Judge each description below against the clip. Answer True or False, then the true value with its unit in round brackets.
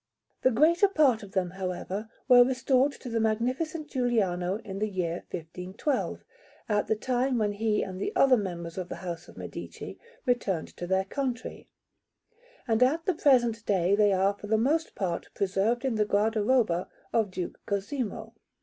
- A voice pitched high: True (215 Hz)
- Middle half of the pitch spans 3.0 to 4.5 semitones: False (4.9 semitones)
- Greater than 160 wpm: True (170 wpm)